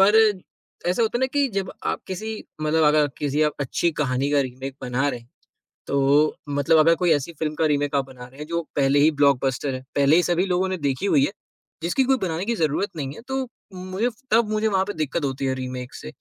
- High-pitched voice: No, medium, 150 Hz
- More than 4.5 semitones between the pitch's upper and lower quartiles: Yes, average, 5.3 semitones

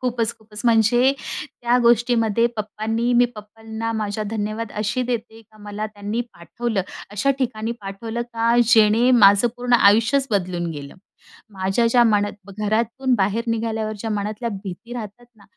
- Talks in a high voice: Yes, high, 220 Hz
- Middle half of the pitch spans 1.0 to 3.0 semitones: Yes, narrow, 2.4 semitones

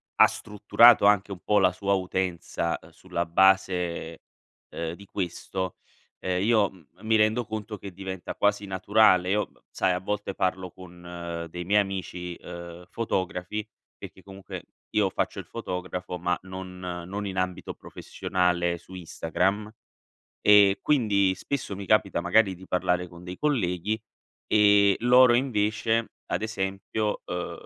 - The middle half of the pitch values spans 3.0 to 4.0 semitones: No, narrow, 2.6 semitones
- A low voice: Yes, very low, 95 Hz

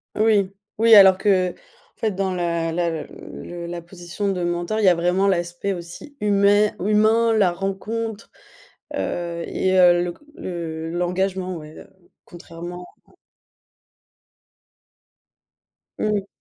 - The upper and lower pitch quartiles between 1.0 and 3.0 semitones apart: Yes, average, 2.7 semitones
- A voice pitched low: No, medium, 185 Hz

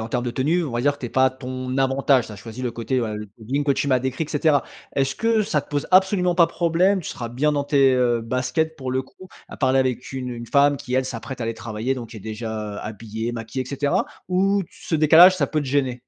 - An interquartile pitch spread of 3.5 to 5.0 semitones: Yes, average, 3.8 semitones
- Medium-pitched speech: No, low, 130 Hz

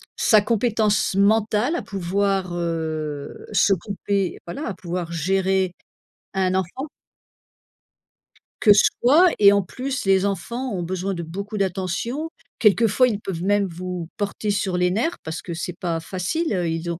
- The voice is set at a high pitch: Yes, high, 195 Hz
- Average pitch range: Yes, average, 3.2 semitones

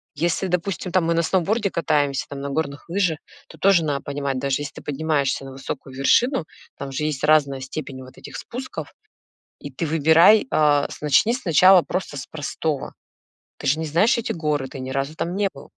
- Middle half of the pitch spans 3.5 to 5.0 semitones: Yes, average, 4.0 semitones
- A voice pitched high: No, medium, 155 Hz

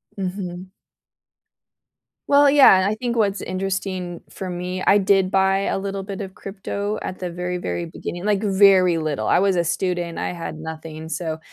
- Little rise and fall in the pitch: Yes, narrow, 2.0 semitones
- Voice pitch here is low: No, medium, 185 Hz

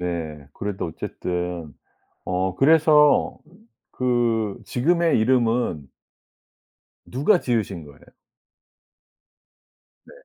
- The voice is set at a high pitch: No, low, 110 Hz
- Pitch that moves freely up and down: Yes, wide, 6.7 semitones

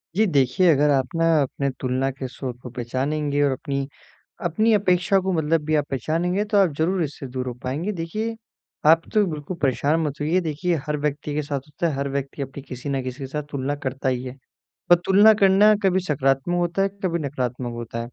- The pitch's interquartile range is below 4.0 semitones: No, average, 4.6 semitones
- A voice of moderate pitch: Yes, medium, 150 Hz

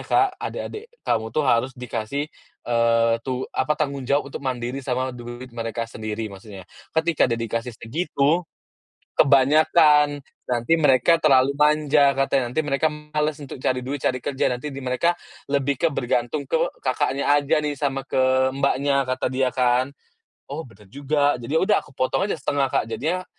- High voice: No, low, 135 Hz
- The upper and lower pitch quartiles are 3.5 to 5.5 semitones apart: No, average, 3.0 semitones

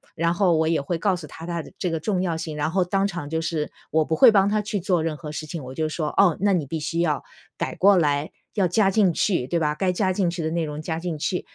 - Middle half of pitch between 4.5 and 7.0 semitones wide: No, average, 3.1 semitones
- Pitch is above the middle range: No, medium, 170 Hz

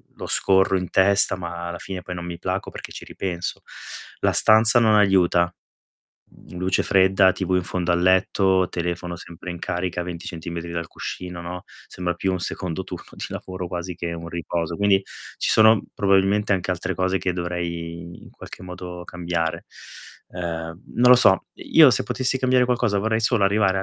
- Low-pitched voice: Yes, very low, 90 Hz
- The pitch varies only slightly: Yes, narrow, 1.9 semitones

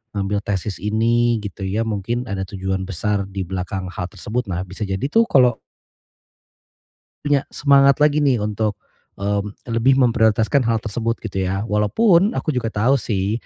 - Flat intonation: No, average, 4.0 semitones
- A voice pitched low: Yes, low, 105 Hz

